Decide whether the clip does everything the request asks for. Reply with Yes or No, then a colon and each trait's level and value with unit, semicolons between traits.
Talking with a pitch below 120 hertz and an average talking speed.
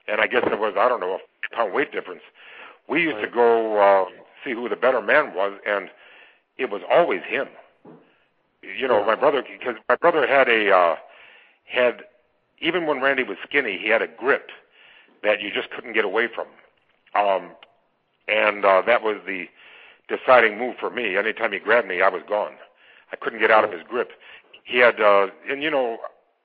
No: low, 125 Hz; average, 195 wpm